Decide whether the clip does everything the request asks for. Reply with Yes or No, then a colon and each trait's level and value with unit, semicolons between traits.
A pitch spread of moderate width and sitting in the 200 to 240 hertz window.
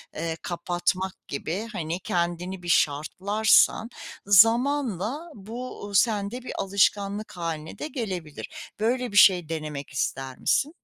No: average, 4.8 semitones; high, 190 Hz